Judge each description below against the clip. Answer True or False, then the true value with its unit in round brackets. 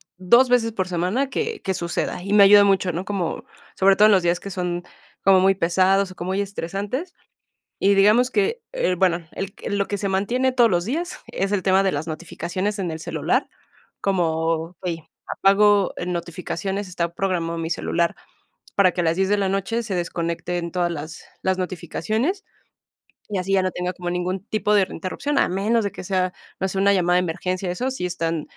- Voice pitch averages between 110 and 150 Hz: False (190 Hz)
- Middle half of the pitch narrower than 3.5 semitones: True (2.5 semitones)